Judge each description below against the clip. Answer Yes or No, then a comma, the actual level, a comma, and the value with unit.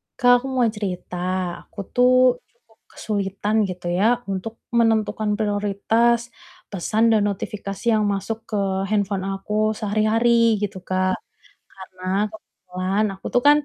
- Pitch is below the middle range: No, high, 210 Hz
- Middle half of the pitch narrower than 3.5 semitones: Yes, average, 2.8 semitones